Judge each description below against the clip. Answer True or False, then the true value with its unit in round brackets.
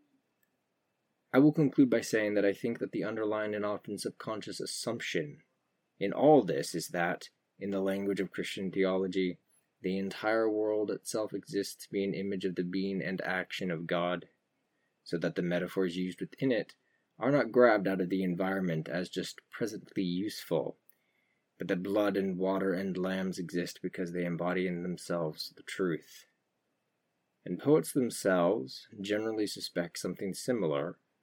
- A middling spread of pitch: False (2.3 semitones)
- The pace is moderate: True (160 wpm)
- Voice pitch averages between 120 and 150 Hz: False (95 Hz)